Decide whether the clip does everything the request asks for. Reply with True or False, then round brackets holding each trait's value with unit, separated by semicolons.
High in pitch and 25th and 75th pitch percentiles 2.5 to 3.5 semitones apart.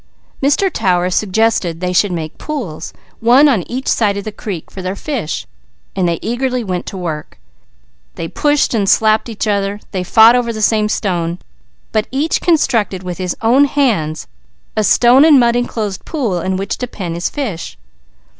False (215 Hz; 5.2 semitones)